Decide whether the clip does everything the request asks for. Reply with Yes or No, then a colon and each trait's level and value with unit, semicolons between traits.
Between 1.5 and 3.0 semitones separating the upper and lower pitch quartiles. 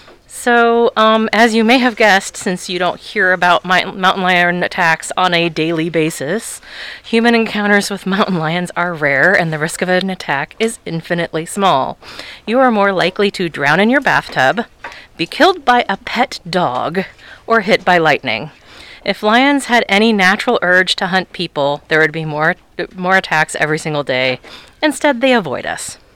No: average, 5.0 semitones